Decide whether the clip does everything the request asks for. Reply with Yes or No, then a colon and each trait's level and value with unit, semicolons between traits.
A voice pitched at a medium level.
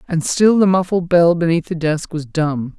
Yes: medium, 170 Hz